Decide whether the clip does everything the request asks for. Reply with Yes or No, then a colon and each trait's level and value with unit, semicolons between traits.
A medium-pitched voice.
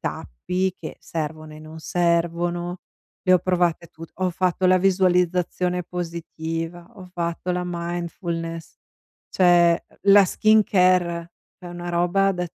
Yes: medium, 175 Hz